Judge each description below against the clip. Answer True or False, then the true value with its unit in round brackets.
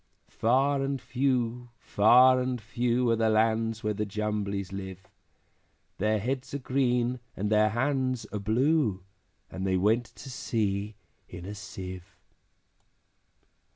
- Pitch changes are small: False (3.8 semitones)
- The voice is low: True (115 Hz)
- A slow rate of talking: True (130 wpm)